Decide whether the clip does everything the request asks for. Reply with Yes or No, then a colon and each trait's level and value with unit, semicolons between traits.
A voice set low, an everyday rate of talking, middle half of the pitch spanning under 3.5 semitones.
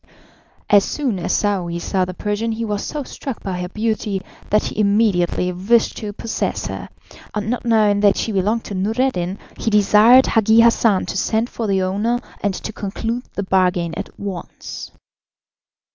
No: high, 205 Hz; average, 170 wpm; average, 2.9 semitones